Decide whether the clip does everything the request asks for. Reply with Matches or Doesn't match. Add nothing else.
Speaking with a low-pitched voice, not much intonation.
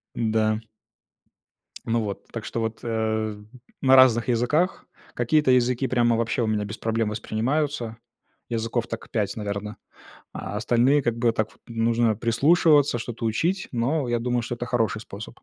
Matches